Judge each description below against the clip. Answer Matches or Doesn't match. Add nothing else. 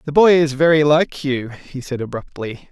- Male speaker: Matches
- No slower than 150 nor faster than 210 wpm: Matches